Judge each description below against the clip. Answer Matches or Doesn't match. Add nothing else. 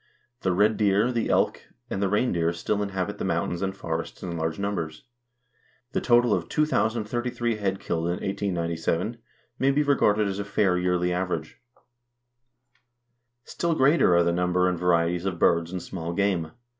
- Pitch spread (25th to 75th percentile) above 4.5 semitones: Doesn't match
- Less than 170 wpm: Matches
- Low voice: Matches